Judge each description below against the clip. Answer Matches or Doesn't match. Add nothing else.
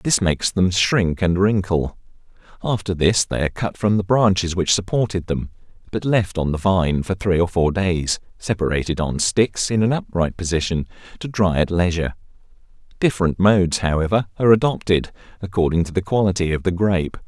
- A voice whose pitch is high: Doesn't match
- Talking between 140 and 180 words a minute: Matches